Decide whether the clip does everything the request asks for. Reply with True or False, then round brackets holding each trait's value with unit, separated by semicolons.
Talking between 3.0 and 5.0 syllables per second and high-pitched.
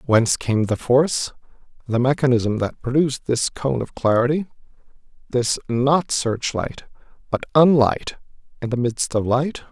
False (4.5 syllables/s; 125 Hz)